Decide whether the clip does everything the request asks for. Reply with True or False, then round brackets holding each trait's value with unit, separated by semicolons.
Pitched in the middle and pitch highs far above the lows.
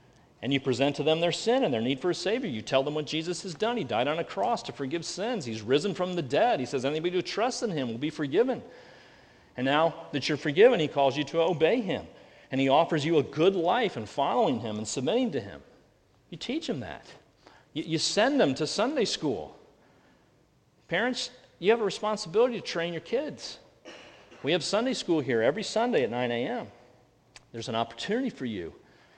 True (165 Hz; 6.7 semitones)